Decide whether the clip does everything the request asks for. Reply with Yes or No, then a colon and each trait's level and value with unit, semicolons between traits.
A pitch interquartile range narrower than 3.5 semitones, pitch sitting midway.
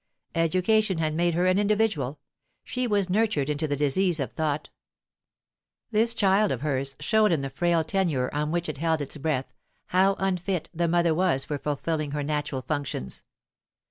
No: average, 4.6 semitones; medium, 165 Hz